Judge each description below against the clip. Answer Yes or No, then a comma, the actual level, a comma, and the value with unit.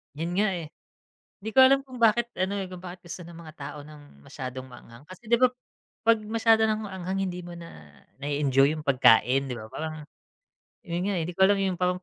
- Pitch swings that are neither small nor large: No, wide, 6.0 semitones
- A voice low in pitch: No, medium, 175 Hz